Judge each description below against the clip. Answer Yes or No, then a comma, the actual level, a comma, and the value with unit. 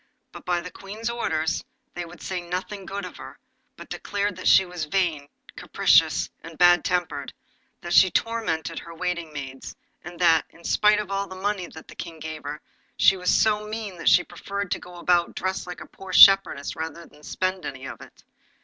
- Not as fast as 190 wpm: No, average, 200 wpm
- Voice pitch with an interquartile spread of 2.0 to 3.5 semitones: Yes, average, 2.8 semitones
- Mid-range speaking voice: Yes, medium, 180 Hz